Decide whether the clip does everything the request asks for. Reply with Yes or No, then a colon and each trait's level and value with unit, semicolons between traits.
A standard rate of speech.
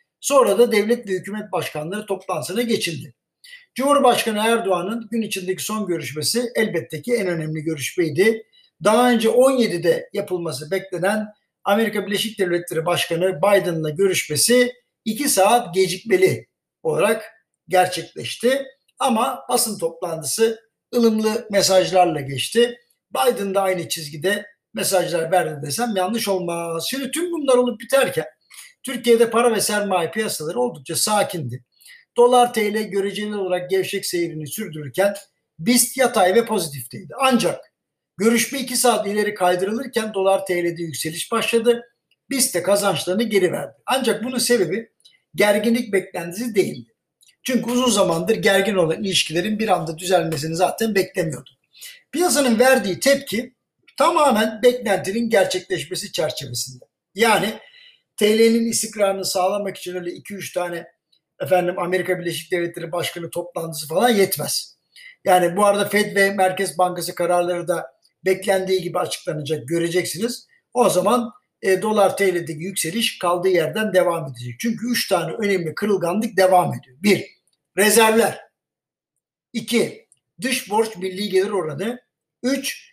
Yes: average, 120 wpm